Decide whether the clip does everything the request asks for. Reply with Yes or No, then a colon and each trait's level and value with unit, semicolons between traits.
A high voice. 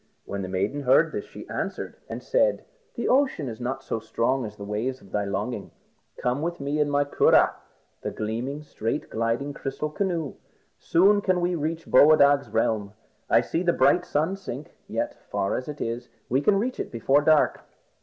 No: medium, 140 Hz